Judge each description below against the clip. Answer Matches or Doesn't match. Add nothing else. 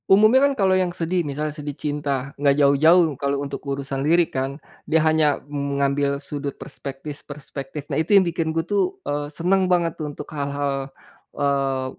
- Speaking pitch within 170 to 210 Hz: Doesn't match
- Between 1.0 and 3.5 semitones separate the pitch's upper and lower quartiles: Matches